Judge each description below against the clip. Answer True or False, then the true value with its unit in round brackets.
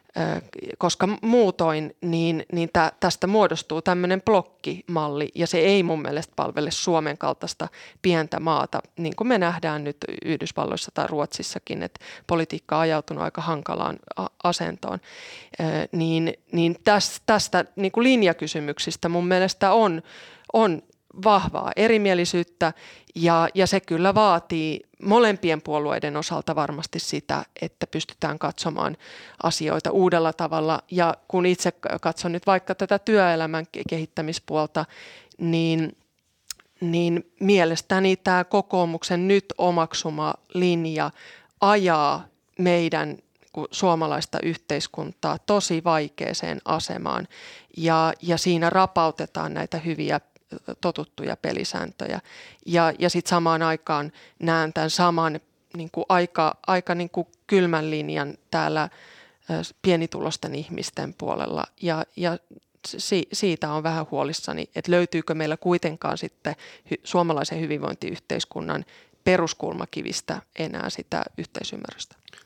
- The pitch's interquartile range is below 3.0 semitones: True (2.5 semitones)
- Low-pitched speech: False (170 Hz)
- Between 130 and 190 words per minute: False (110 wpm)